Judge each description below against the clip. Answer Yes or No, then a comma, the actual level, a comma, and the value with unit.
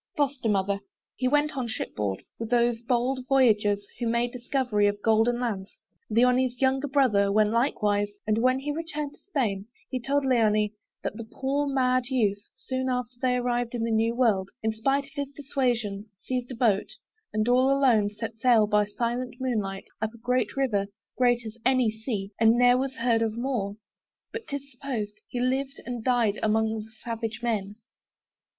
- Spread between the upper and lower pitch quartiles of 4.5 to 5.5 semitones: No, average, 3.2 semitones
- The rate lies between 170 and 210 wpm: Yes, average, 180 wpm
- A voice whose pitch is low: No, high, 240 Hz